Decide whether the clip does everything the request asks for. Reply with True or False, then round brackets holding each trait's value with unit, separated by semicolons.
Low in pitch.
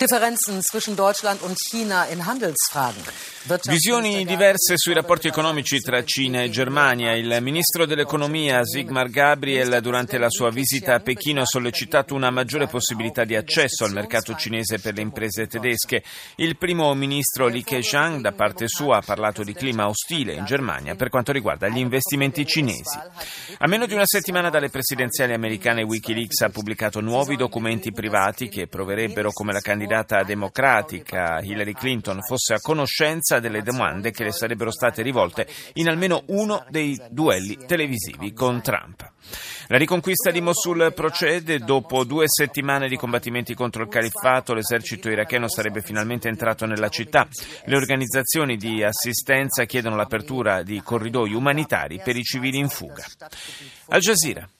True (125 Hz)